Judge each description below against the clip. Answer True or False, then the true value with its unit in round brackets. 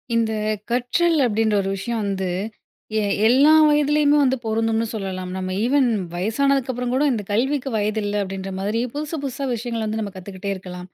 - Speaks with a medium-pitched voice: False (225 Hz)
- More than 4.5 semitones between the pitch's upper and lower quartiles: True (4.9 semitones)